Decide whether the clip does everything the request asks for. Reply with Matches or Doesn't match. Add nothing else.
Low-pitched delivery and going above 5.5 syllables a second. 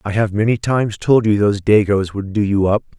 Matches